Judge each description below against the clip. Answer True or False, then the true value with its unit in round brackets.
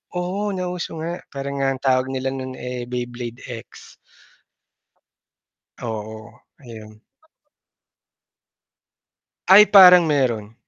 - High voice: False (130 Hz)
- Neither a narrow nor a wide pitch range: False (6.4 semitones)